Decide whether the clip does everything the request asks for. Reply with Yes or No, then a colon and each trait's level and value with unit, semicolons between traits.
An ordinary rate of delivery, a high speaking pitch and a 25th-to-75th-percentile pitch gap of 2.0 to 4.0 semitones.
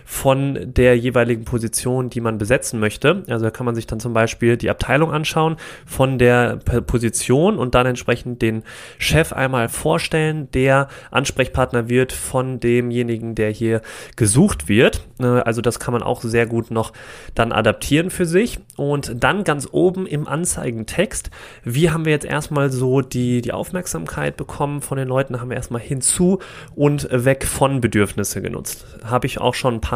No: average, 170 wpm; low, 125 Hz; average, 3.0 semitones